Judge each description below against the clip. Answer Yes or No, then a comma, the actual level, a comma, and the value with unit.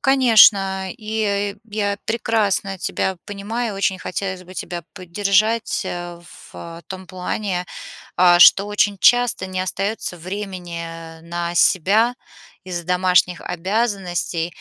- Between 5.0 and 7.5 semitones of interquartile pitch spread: No, average, 2.8 semitones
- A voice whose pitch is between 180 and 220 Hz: Yes, high, 190 Hz